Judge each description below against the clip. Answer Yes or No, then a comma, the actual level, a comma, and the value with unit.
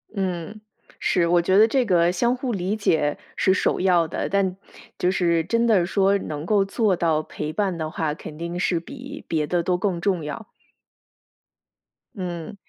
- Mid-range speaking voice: Yes, medium, 180 Hz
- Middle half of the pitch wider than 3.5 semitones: No, average, 3.2 semitones